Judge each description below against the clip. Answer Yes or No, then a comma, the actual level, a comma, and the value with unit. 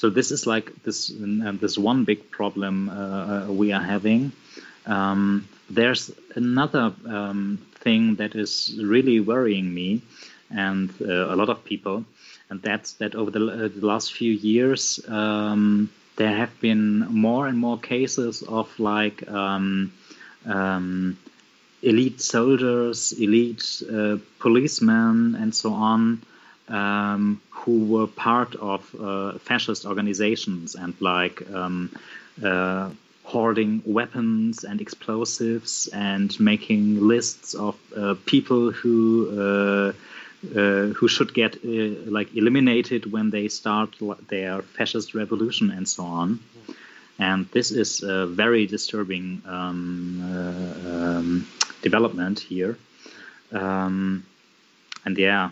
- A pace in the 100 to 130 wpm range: Yes, slow, 125 wpm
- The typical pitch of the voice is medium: No, low, 105 Hz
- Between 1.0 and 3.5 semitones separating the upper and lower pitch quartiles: Yes, average, 2.7 semitones